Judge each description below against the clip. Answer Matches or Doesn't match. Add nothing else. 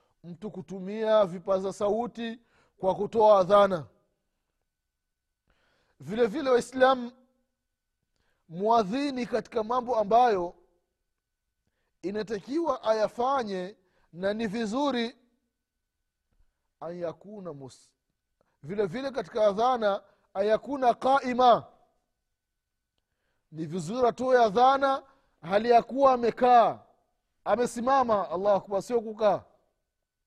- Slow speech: Matches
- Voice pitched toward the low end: Doesn't match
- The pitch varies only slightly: Doesn't match